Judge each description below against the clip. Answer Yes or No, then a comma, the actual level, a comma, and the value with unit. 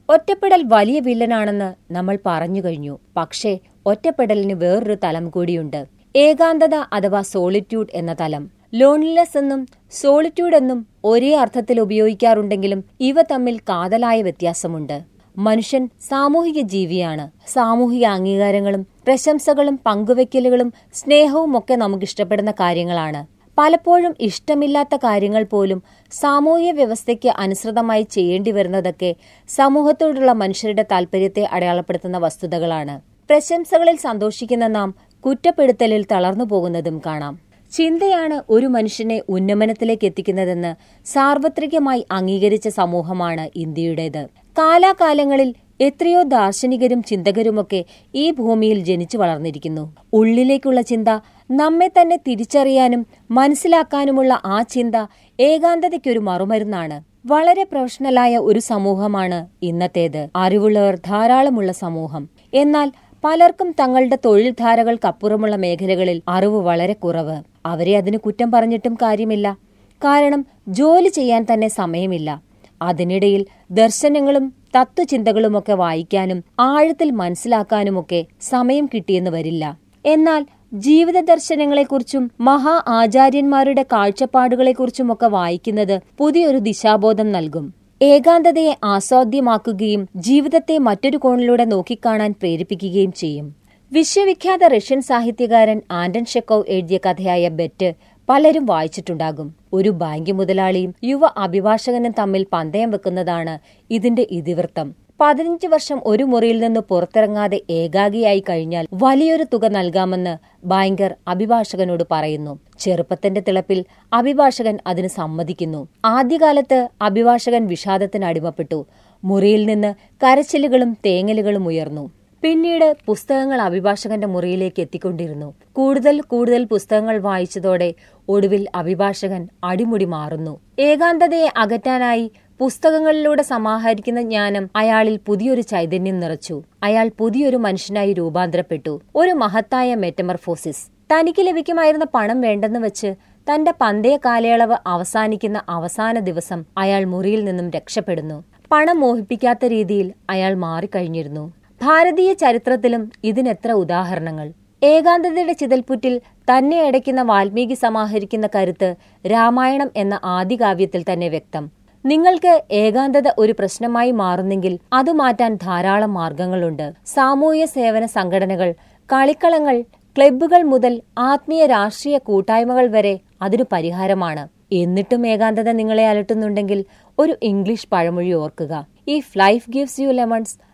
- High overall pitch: Yes, high, 220 Hz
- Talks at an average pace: Yes, average, 95 wpm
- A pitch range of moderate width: No, wide, 6.1 semitones